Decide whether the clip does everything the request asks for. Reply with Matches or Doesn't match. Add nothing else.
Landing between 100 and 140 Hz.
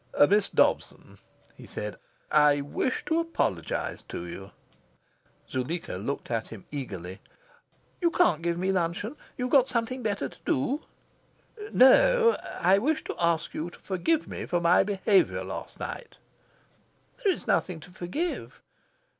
Doesn't match